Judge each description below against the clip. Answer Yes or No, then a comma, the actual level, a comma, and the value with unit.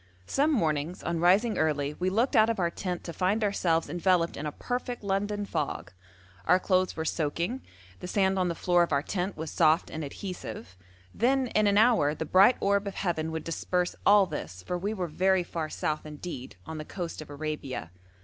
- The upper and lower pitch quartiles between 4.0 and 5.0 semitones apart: Yes, average, 4.4 semitones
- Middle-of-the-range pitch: Yes, medium, 180 Hz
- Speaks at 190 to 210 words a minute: Yes, average, 200 wpm